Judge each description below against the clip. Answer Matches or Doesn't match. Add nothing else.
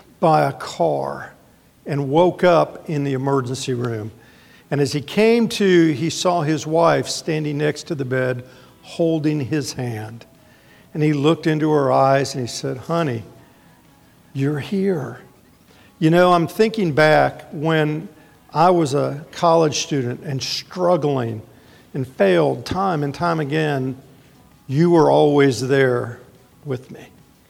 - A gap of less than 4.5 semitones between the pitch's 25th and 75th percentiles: Matches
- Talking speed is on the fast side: Doesn't match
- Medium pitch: Matches